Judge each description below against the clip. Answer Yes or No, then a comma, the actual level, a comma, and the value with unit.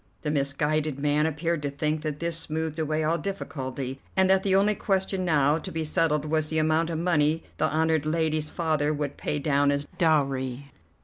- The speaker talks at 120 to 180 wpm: No, average, 190 wpm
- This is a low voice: No, medium, 155 Hz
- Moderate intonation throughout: No, narrow, 1.9 semitones